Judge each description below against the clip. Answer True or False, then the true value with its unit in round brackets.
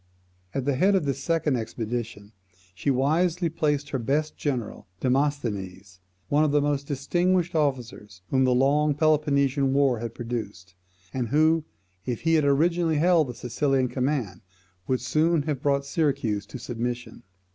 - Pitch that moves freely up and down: False (3.8 semitones)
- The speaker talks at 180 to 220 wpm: False (150 wpm)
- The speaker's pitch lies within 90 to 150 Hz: True (140 Hz)